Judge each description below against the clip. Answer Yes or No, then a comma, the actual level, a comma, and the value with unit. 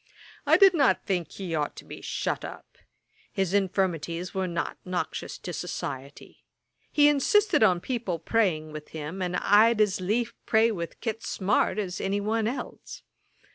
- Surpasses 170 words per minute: No, average, 160 wpm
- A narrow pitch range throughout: No, average, 4.4 semitones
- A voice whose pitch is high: Yes, high, 195 Hz